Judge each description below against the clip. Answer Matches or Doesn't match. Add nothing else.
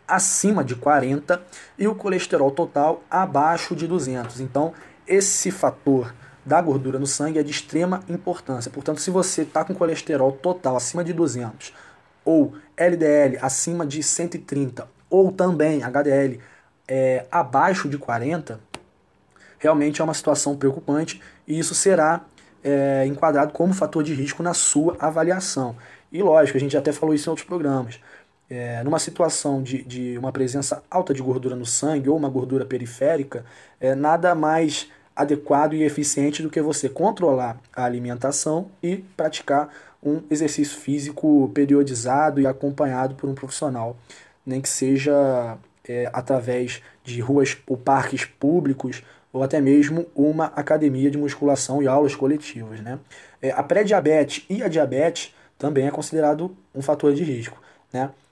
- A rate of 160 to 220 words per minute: Doesn't match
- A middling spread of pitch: Matches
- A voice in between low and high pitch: Matches